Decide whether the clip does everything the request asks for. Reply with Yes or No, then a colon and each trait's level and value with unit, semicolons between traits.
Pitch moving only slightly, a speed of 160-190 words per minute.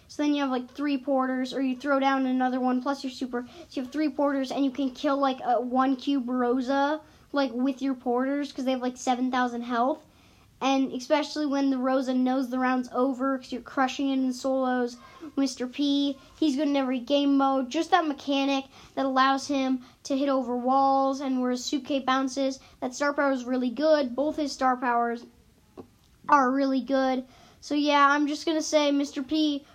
No: narrow, 1.7 semitones; average, 200 wpm